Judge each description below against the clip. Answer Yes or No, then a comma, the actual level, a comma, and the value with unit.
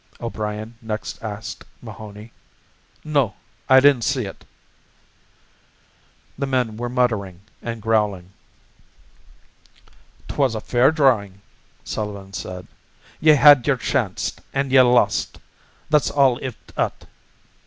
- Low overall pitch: Yes, low, 115 Hz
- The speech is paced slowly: Yes, slow, 110 wpm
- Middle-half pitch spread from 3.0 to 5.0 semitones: Yes, average, 4.1 semitones